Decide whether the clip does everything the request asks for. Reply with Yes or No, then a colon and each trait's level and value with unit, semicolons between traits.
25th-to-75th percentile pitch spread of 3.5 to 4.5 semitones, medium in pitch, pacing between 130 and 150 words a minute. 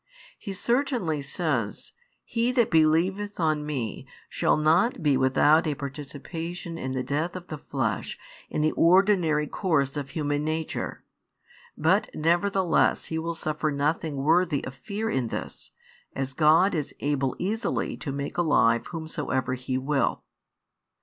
Yes: average, 3.8 semitones; medium, 155 Hz; average, 140 wpm